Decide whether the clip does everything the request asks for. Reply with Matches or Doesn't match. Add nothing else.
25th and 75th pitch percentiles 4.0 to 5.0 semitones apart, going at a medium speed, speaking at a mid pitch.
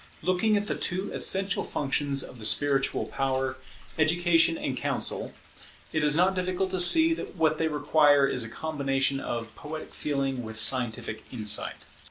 Matches